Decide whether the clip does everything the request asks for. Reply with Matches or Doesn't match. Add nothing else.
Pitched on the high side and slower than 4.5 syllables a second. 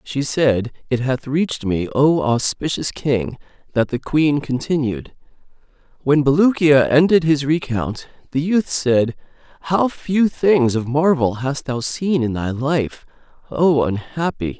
Doesn't match